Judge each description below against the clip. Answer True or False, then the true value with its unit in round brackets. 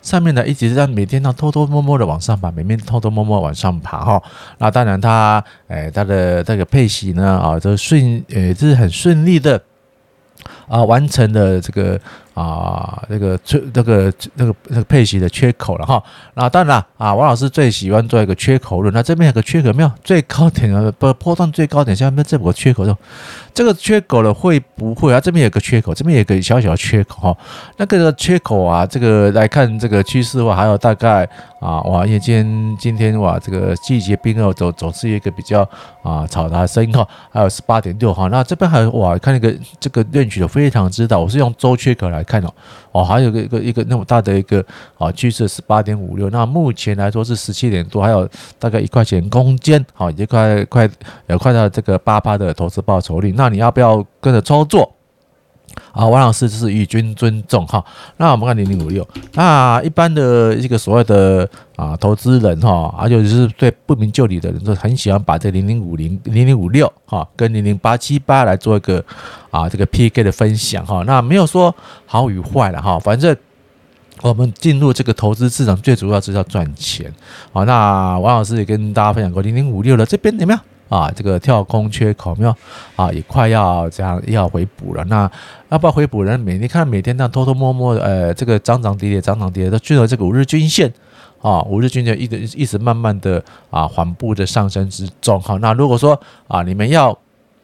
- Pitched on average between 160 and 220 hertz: False (110 Hz)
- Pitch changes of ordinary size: True (4.6 semitones)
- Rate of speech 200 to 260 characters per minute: False (310 characters per minute)